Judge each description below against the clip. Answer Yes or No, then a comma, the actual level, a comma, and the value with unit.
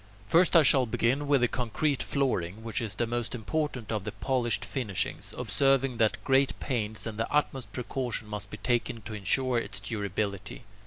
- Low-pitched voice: Yes, low, 115 Hz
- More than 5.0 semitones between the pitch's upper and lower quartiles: No, average, 3.9 semitones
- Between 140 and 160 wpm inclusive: No, average, 175 wpm